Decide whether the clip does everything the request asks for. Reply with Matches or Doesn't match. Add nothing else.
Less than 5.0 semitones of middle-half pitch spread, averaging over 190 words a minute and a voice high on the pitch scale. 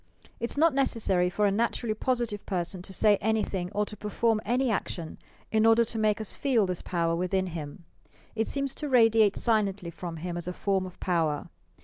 Matches